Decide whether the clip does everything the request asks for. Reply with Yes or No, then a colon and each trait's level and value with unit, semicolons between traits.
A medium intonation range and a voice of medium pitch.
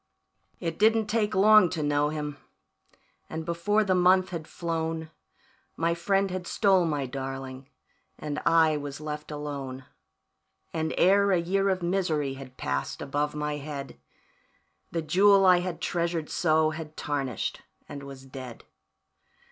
Yes: average, 3.9 semitones; medium, 160 Hz